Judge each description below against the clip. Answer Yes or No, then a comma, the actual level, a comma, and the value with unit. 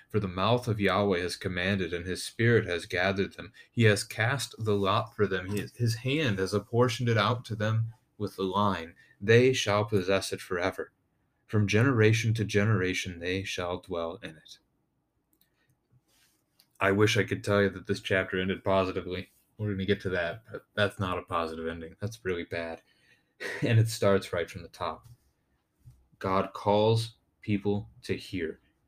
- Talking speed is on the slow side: No, average, 170 wpm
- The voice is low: Yes, low, 100 Hz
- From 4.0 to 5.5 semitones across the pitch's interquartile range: No, average, 2.8 semitones